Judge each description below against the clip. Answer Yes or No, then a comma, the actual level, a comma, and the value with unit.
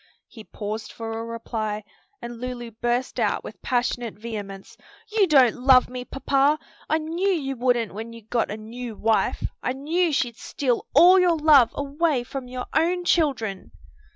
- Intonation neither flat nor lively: Yes, average, 4.3 semitones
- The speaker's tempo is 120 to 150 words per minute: No, average, 165 wpm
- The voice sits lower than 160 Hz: No, very high, 250 Hz